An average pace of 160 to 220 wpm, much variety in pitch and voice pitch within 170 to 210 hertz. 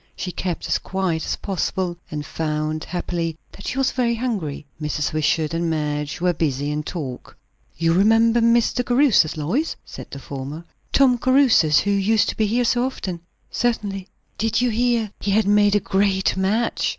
Yes: average, 175 wpm; wide, 6.6 semitones; high, 190 Hz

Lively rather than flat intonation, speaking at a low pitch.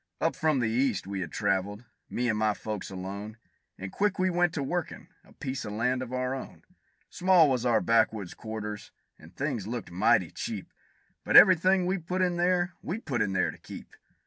Yes: wide, 8.7 semitones; low, 125 Hz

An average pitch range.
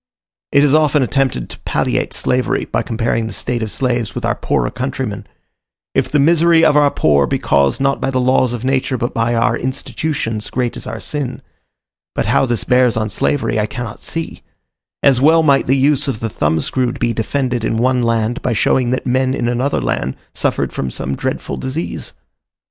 Yes: average, 3.2 semitones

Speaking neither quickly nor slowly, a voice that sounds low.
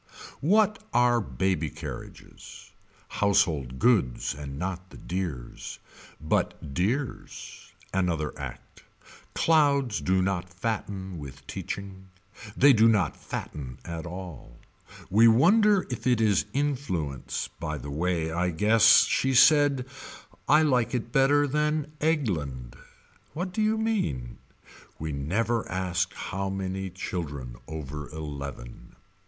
No: slow, 115 wpm; very low, 95 Hz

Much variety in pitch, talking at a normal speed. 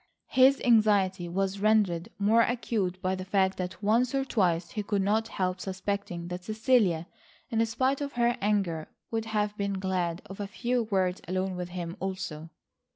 No: average, 3.3 semitones; average, 170 wpm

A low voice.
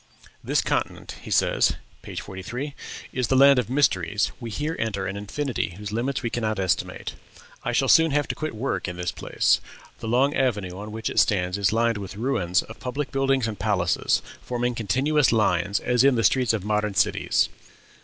Yes: low, 115 Hz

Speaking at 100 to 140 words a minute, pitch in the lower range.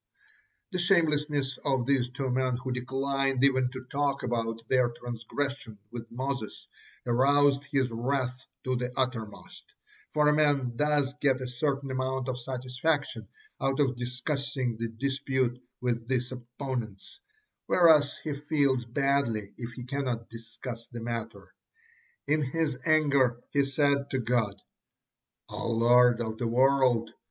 Yes: slow, 135 wpm; low, 130 Hz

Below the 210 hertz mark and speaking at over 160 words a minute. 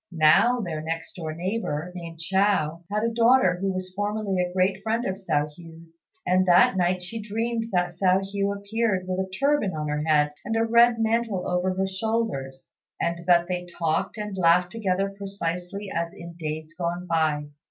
Yes: medium, 185 Hz; average, 185 wpm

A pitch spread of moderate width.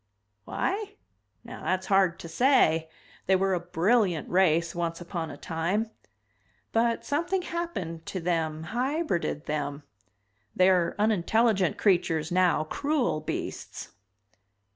No: wide, 5.7 semitones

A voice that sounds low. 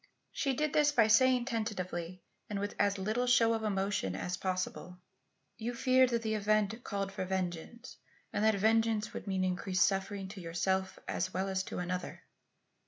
No: high, 200 Hz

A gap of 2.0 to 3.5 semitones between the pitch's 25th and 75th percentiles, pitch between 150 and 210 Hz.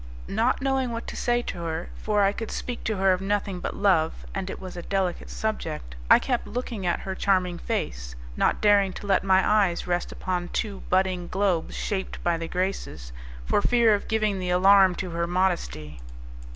Yes: average, 2.8 semitones; high, 190 Hz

